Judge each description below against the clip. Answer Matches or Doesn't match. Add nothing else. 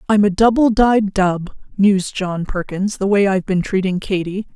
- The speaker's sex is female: Matches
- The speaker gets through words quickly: Doesn't match